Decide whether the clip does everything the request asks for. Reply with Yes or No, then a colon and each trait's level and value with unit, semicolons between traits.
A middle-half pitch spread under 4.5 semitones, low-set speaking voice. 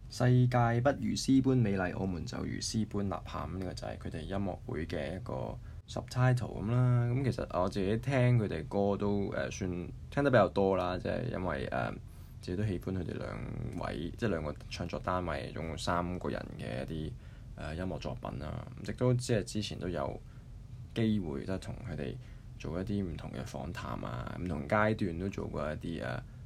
No: average, 5.2 semitones; low, 105 Hz